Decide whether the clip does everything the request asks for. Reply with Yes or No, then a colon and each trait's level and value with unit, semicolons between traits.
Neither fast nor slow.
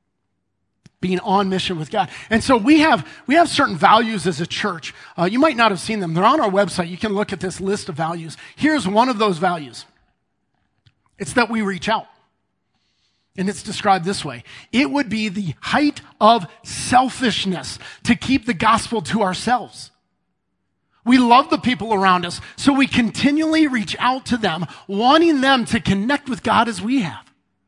Yes: average, 185 wpm